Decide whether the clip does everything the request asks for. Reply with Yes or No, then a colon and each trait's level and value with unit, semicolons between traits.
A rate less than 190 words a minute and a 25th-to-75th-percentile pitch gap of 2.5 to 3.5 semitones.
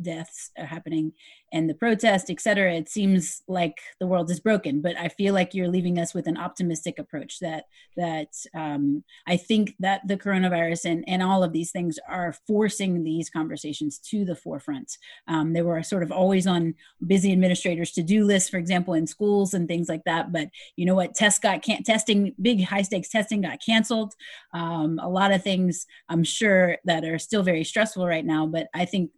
No: average, 200 wpm; average, 3.1 semitones